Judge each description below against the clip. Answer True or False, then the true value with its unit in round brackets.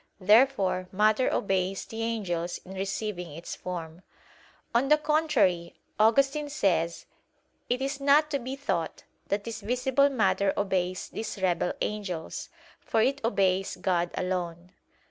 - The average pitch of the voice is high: True (205 Hz)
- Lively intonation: True (6.1 semitones)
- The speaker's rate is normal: False (130 wpm)